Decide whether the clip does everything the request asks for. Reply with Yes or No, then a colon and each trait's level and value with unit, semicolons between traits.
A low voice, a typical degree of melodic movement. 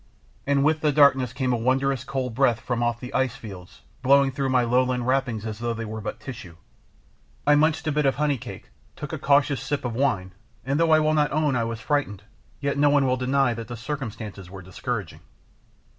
Yes: low, 130 Hz; average, 3.4 semitones